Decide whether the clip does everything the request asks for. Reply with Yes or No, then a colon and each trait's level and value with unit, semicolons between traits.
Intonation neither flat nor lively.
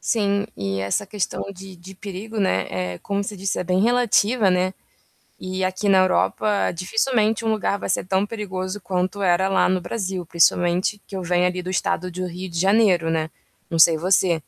No: narrow, 2.2 semitones